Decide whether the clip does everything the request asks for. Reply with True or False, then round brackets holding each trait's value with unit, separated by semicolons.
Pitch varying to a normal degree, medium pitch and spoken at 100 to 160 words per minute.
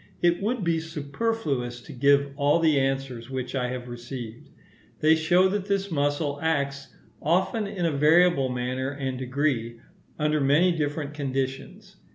True (4.1 semitones; 145 Hz; 150 wpm)